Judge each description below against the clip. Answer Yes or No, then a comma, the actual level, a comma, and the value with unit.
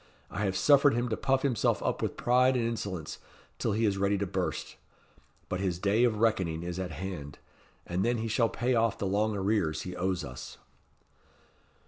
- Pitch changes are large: No, average, 4.1 semitones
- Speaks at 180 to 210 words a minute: Yes, average, 190 wpm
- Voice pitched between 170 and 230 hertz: No, low, 100 Hz